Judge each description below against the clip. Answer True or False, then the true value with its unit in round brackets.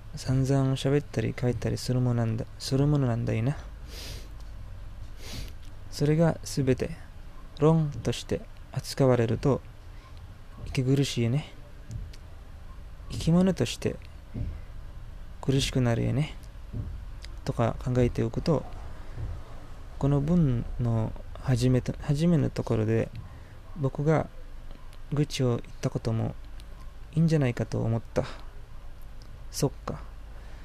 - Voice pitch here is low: True (115 Hz)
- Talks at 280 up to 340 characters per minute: False (205 characters per minute)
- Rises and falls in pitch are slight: False (5.4 semitones)